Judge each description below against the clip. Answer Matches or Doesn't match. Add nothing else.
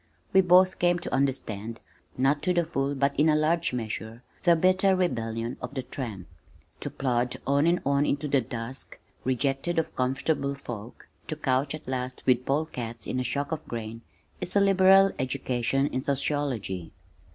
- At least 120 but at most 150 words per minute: Doesn't match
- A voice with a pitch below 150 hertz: Matches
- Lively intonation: Doesn't match